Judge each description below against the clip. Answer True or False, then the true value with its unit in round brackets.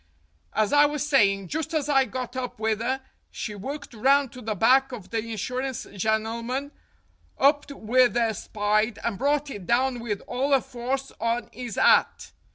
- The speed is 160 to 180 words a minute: True (170 wpm)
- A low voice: False (245 Hz)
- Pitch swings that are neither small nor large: True (3.7 semitones)